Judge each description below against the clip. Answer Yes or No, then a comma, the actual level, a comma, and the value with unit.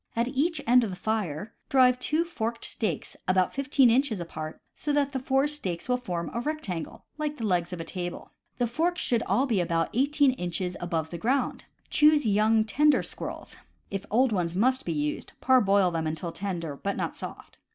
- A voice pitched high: Yes, high, 225 Hz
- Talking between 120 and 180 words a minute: No, average, 195 wpm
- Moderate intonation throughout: No, wide, 7.1 semitones